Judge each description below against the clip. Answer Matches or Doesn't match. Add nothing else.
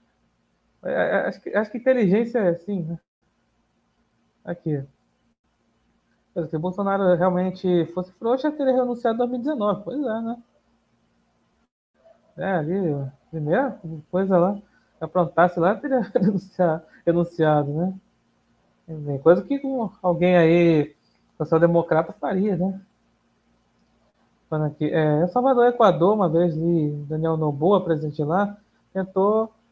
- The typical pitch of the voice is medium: Matches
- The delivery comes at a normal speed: Doesn't match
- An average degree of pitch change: Matches